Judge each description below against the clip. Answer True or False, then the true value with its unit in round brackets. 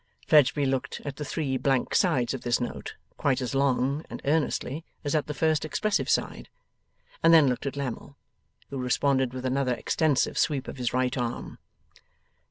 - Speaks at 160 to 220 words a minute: True (175 wpm)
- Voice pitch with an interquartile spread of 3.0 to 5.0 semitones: False (2.6 semitones)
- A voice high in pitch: False (135 Hz)